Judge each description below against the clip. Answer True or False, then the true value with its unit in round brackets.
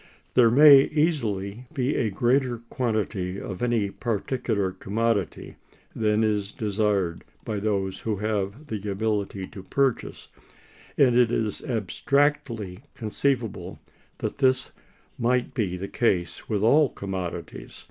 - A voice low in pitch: True (110 Hz)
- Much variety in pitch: False (3.9 semitones)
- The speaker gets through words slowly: True (120 wpm)